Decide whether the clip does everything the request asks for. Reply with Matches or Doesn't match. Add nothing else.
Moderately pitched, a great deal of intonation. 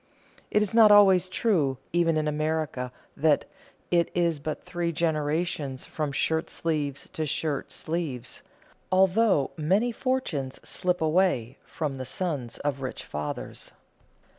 Doesn't match